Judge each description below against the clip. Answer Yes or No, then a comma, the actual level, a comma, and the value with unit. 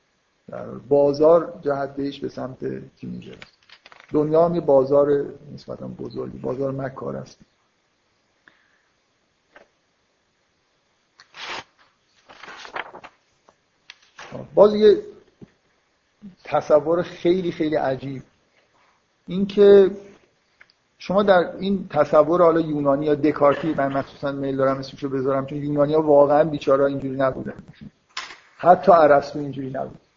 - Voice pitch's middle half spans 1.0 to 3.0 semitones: No, average, 4.0 semitones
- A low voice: No, medium, 145 Hz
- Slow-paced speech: Yes, slow, 95 wpm